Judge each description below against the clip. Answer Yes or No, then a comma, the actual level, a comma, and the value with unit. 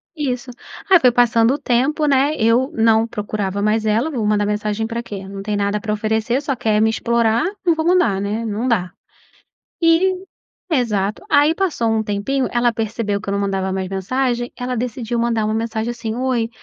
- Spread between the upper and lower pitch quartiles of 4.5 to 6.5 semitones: No, average, 3.3 semitones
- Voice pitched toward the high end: Yes, high, 230 Hz